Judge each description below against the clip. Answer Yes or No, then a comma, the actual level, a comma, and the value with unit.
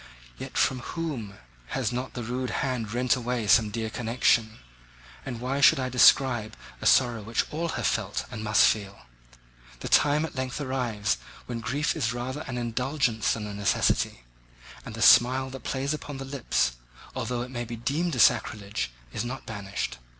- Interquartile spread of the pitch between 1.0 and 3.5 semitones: Yes, average, 3.1 semitones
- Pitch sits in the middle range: No, low, 125 Hz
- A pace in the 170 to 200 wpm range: Yes, average, 175 wpm